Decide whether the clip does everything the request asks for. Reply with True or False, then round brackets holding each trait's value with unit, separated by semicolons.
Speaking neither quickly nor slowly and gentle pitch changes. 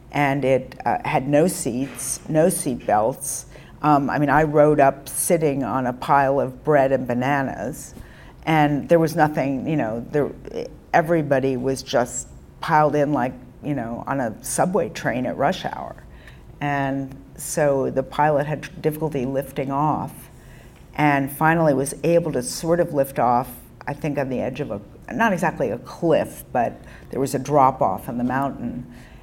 True (170 wpm; 2.3 semitones)